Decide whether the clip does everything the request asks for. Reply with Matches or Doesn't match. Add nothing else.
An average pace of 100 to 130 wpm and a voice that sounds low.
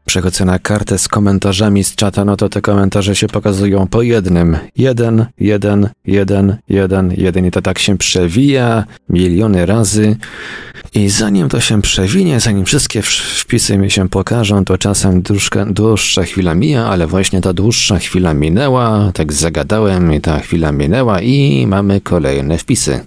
Doesn't match